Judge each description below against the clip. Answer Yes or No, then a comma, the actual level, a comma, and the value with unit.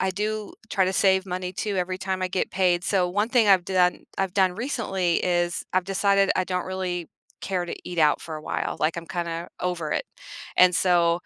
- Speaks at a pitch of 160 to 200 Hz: Yes, medium, 185 Hz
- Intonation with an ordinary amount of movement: No, narrow, 1.6 semitones